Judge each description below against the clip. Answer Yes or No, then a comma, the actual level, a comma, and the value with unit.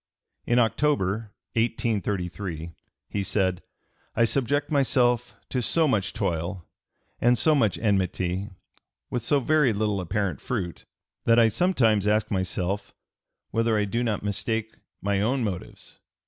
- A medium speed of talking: No, slow, 130 wpm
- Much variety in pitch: No, average, 3.7 semitones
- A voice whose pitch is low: Yes, low, 110 Hz